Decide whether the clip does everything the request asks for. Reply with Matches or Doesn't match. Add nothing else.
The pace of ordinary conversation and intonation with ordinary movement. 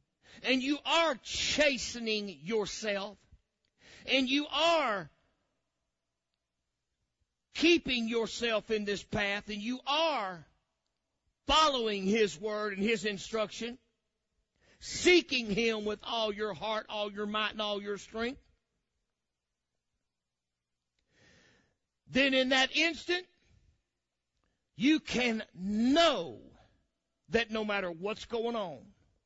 Doesn't match